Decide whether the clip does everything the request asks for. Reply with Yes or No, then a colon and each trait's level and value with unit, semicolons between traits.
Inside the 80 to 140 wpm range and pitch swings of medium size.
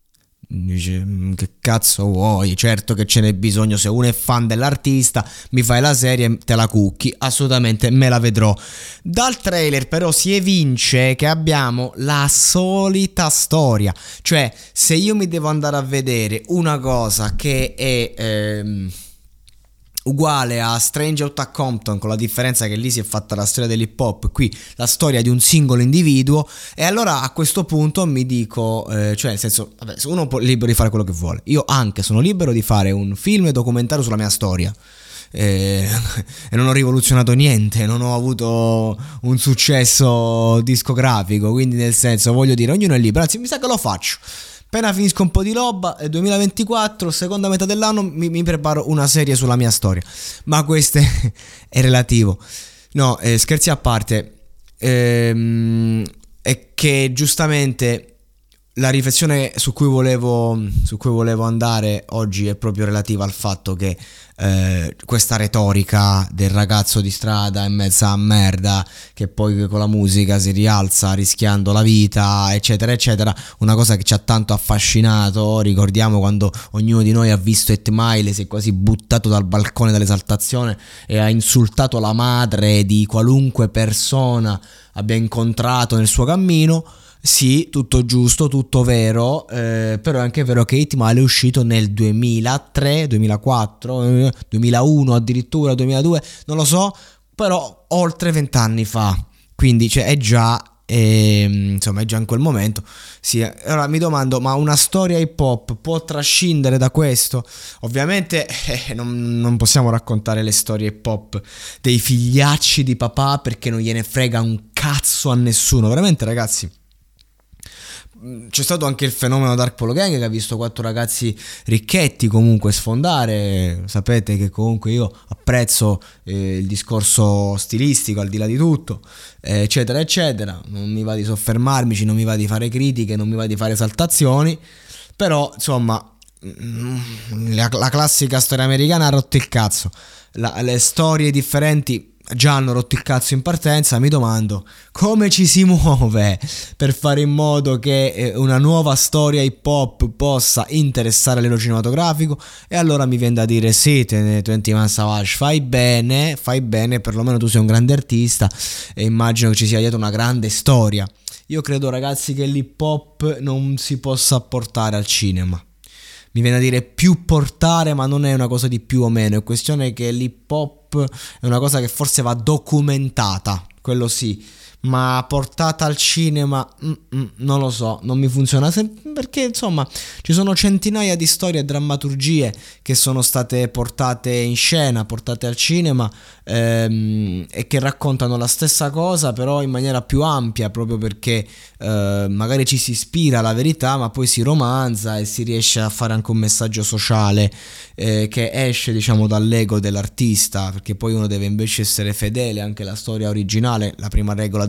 No: average, 160 wpm; average, 4.4 semitones